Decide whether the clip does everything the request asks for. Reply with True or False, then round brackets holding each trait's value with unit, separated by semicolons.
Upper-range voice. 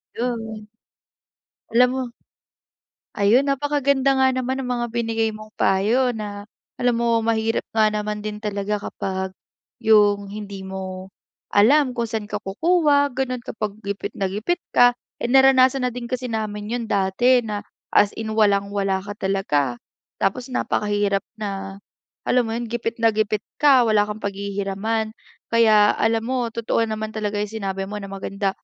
True (215 Hz)